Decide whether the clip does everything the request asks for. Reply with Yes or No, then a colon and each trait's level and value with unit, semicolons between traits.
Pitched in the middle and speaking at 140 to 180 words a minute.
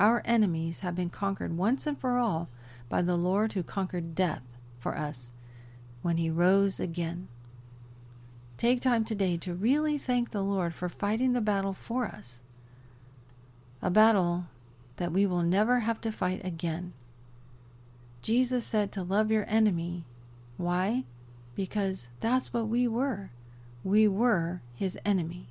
Yes: medium, 180 Hz; average, 145 wpm